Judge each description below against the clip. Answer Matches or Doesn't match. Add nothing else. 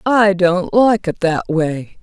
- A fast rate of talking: Doesn't match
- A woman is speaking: Matches